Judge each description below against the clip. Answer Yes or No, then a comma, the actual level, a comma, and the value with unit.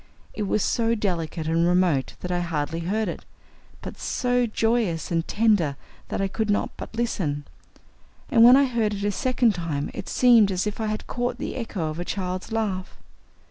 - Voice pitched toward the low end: No, high, 200 Hz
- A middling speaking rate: Yes, average, 185 wpm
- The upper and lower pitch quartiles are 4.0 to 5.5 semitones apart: Yes, average, 5.0 semitones